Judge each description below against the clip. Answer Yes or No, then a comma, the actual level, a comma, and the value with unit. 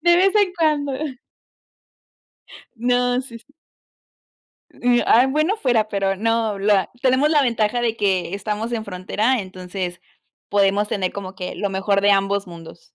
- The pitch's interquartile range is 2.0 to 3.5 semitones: No, average, 4.5 semitones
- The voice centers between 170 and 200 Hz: No, high, 215 Hz